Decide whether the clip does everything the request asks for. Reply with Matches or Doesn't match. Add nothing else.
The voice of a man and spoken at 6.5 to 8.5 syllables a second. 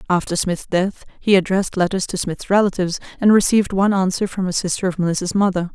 Doesn't match